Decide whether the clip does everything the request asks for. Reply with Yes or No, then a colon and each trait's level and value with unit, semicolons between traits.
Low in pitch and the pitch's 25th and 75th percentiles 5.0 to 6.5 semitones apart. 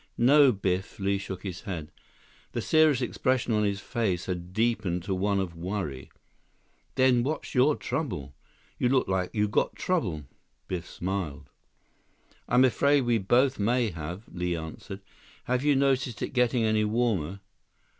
Yes: low, 105 Hz; wide, 5.5 semitones